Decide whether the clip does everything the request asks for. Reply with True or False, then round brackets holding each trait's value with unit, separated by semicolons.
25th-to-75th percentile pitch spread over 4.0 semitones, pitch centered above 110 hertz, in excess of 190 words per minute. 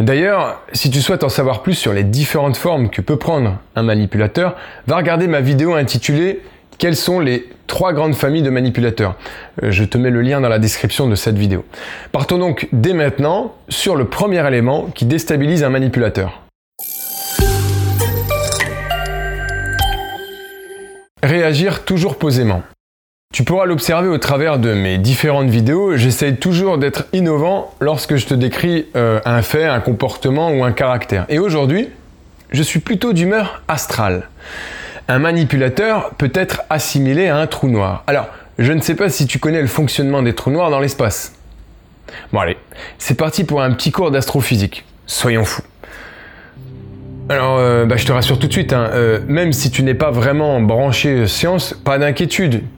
False (5.4 semitones; 135 Hz; 165 wpm)